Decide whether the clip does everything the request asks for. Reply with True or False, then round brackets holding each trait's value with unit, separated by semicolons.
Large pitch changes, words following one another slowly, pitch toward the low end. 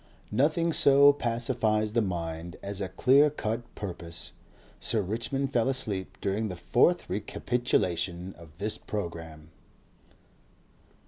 True (5.8 semitones; 115 wpm; 105 Hz)